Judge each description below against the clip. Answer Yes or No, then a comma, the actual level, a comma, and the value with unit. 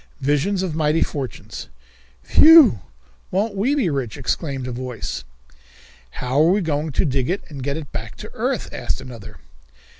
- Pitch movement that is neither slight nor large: No, wide, 6.1 semitones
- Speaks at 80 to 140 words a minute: No, average, 160 wpm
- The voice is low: No, medium, 145 Hz